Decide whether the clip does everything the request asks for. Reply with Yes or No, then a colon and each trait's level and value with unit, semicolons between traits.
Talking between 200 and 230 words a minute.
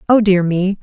Yes: fast, 220 wpm